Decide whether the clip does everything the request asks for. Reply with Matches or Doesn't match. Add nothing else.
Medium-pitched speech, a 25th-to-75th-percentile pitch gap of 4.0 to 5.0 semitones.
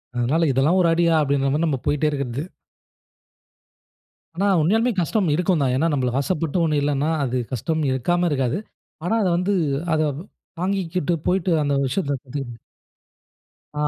Matches